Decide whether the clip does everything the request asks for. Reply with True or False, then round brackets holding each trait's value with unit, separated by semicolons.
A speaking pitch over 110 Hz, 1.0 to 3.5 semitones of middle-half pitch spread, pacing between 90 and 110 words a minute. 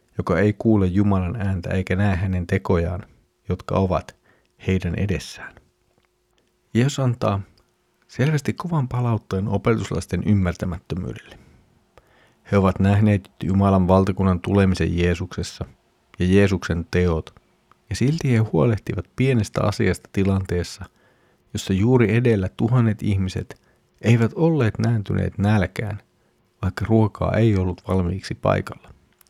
False (100 Hz; 3.2 semitones; 105 wpm)